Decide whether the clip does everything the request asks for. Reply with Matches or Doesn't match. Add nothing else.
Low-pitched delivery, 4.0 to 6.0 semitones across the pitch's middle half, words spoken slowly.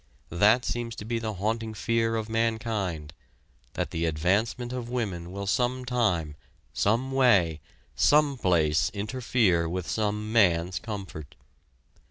Matches